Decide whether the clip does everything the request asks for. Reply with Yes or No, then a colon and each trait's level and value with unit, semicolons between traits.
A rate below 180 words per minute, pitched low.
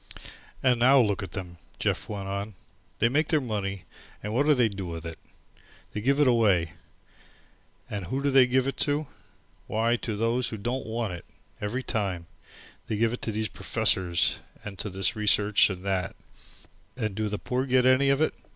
No: average, 190 wpm; low, 110 Hz